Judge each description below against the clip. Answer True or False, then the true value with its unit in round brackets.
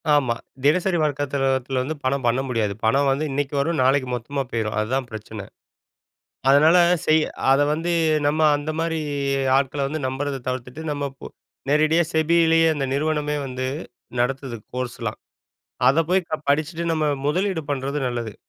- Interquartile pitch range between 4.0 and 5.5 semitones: False (3.3 semitones)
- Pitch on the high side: False (140 Hz)